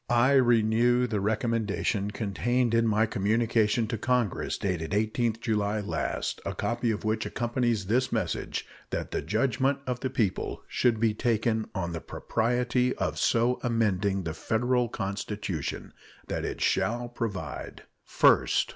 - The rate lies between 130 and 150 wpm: Yes, average, 145 wpm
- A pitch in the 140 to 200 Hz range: No, low, 115 Hz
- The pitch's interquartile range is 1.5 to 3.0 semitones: Yes, average, 2.7 semitones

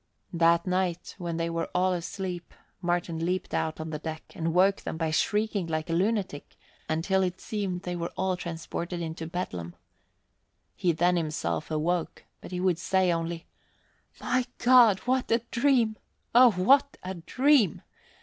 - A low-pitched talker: No, medium, 180 Hz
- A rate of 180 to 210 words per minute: No, average, 160 wpm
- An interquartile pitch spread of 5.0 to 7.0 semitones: No, average, 2.7 semitones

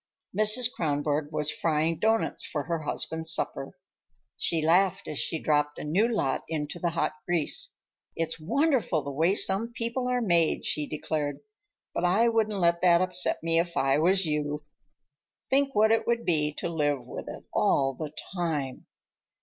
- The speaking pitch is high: No, medium, 165 Hz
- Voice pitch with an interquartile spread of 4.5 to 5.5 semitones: Yes, average, 4.8 semitones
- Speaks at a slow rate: No, average, 165 wpm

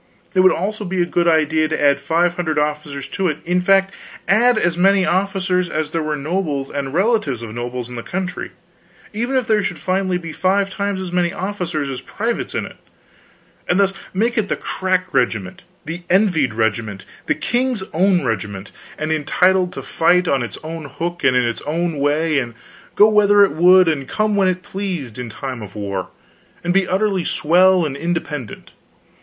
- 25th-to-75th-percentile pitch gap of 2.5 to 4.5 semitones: No, average, 5.0 semitones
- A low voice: No, medium, 175 Hz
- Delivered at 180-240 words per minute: Yes, average, 190 wpm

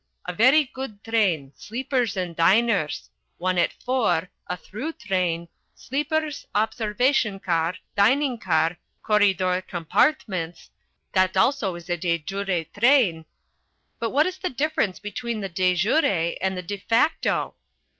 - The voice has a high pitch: Yes, high, 200 Hz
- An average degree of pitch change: No, wide, 5.7 semitones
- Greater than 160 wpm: No, slow, 135 wpm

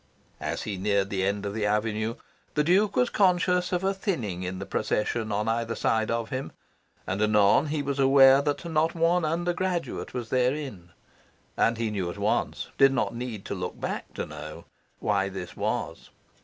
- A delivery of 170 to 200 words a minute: Yes, average, 185 wpm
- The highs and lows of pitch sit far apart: Yes, wide, 7.1 semitones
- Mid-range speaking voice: No, low, 115 Hz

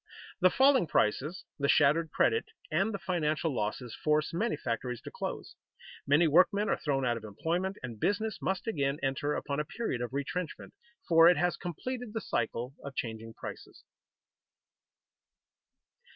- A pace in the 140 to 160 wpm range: Yes, average, 150 wpm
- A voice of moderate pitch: Yes, medium, 155 Hz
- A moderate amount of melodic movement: No, wide, 6.3 semitones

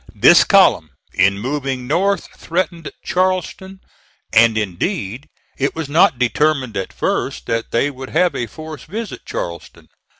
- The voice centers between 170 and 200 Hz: No, medium, 145 Hz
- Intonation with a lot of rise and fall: Yes, wide, 6.9 semitones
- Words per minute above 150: No, slow, 135 wpm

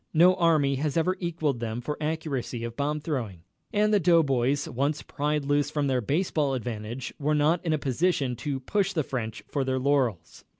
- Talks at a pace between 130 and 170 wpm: No, average, 185 wpm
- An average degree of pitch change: Yes, average, 3.7 semitones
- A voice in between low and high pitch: Yes, medium, 145 Hz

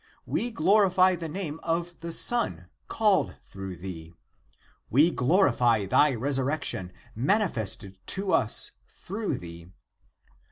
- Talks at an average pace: No, slow, 110 wpm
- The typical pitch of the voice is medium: Yes, medium, 150 Hz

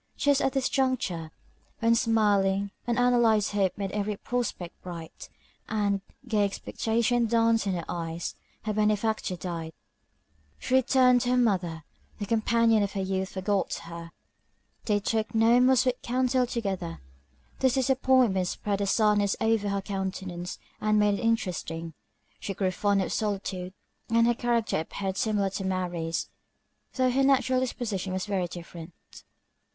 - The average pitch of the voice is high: Yes, high, 210 Hz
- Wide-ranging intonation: No, average, 3.8 semitones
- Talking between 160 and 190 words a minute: No, average, 145 wpm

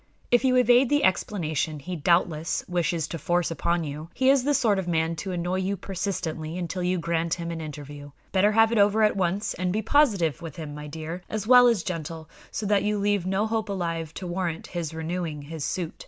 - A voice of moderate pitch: Yes, medium, 175 Hz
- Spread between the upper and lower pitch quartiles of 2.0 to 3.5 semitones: No, average, 4.0 semitones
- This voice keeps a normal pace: No, fast, 215 wpm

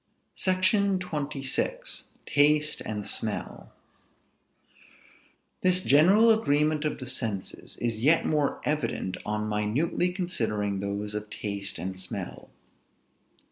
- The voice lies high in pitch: No, medium, 145 Hz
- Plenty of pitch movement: Yes, wide, 8.8 semitones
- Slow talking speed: Yes, slow, 100 wpm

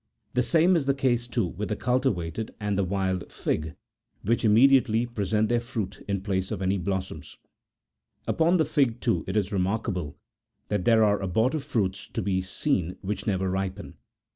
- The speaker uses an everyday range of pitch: Yes, average, 4.2 semitones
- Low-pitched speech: Yes, low, 105 Hz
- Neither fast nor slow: Yes, average, 170 wpm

